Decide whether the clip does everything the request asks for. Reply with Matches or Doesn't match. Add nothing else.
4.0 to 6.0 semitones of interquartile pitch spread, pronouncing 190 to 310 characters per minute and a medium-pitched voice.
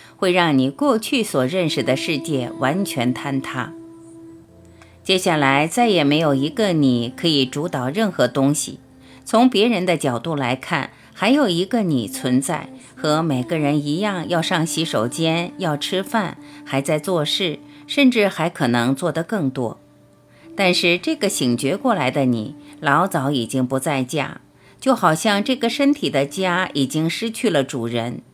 Matches